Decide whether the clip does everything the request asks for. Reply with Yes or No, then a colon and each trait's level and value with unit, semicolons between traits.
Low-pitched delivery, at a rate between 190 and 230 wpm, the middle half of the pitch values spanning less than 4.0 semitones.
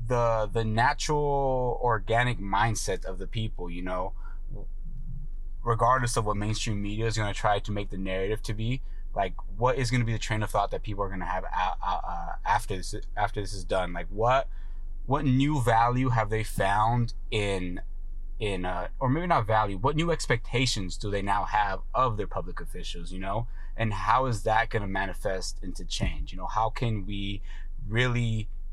Yes: low, 110 Hz; average, 195 wpm; average, 3.5 semitones